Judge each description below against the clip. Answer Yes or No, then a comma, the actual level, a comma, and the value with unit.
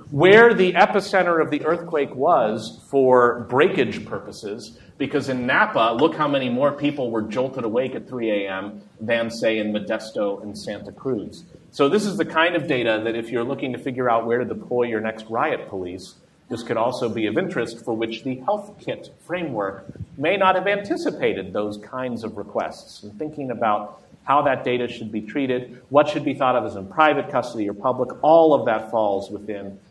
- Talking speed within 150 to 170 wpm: No, average, 195 wpm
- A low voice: Yes, low, 125 Hz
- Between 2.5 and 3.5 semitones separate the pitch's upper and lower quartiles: No, wide, 5.4 semitones